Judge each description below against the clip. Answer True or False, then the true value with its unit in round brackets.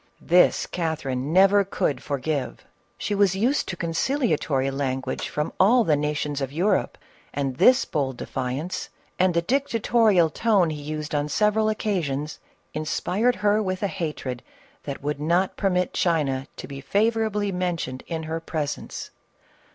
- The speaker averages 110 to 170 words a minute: True (145 wpm)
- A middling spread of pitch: False (5.8 semitones)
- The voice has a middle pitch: True (165 Hz)